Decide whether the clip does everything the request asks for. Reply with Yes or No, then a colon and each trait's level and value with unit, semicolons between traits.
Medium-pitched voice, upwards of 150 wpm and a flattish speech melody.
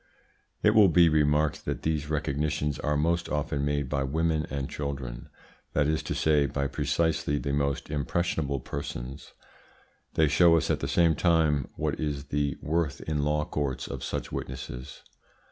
No: very low, 75 Hz; average, 160 wpm; narrow, 1.9 semitones